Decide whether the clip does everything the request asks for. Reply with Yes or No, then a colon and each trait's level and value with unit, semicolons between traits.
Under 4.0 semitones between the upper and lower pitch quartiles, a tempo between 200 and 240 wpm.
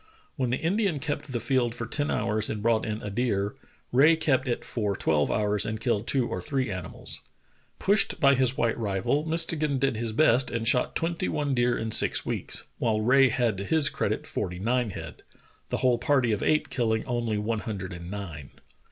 No: average, 4.3 semitones; fast, 205 wpm